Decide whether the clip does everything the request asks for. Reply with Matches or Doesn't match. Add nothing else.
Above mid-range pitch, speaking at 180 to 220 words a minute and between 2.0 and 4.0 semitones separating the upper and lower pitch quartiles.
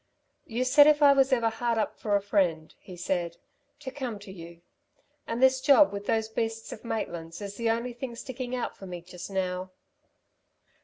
Doesn't match